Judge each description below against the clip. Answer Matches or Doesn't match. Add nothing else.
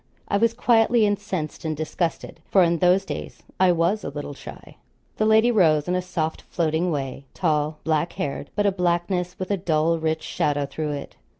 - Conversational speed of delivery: Matches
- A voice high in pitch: Doesn't match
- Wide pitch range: Doesn't match